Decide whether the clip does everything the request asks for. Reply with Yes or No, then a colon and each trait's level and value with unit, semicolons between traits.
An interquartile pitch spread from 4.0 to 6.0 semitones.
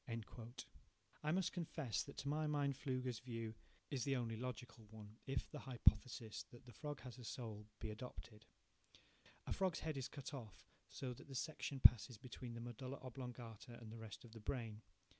No: average, 3.3 semitones